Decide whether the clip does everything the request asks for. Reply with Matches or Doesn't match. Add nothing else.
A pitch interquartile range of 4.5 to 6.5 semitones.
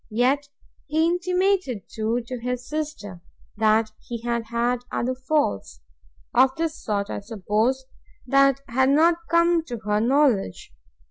Matches